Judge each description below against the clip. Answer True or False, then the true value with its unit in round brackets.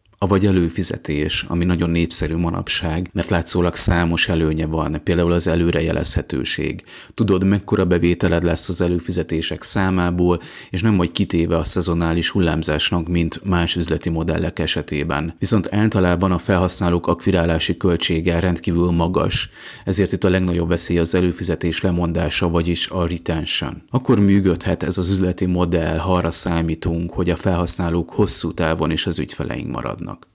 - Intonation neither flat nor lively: False (1.8 semitones)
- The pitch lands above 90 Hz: False (85 Hz)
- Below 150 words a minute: True (140 wpm)